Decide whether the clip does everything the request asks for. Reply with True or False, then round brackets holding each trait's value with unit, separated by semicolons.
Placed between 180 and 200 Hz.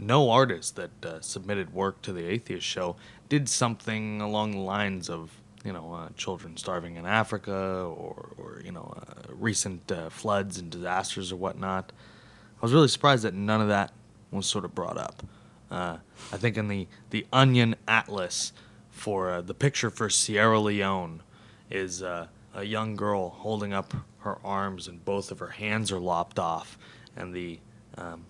False (100 Hz)